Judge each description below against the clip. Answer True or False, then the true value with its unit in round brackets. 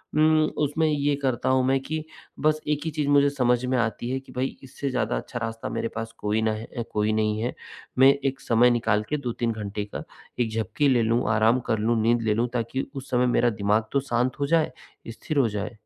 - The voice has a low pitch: True (120 Hz)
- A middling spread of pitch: True (3.6 semitones)